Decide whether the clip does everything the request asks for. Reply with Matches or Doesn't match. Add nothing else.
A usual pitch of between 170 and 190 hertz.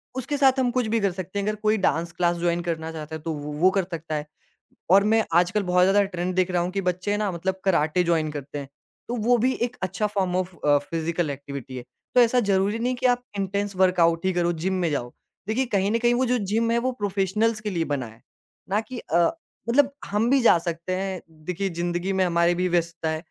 Matches